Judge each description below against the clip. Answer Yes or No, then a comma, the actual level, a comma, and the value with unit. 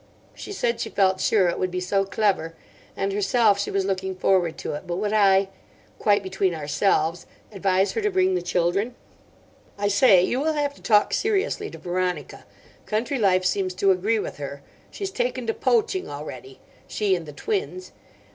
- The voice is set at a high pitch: Yes, high, 195 Hz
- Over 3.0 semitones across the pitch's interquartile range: Yes, average, 4.5 semitones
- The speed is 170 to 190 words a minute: Yes, average, 175 wpm